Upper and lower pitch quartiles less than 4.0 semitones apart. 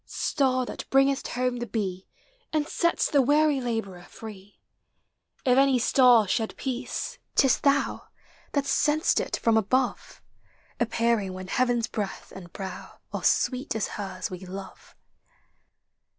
No: average, 5.1 semitones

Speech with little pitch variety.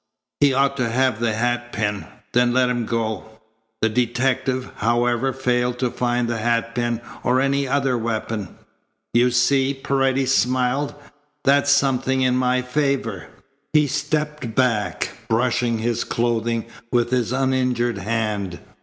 Yes: narrow, 2.3 semitones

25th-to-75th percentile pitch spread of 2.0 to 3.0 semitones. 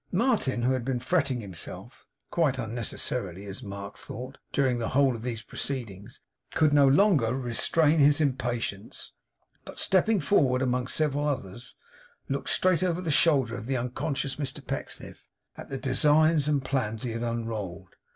No: average, 4.0 semitones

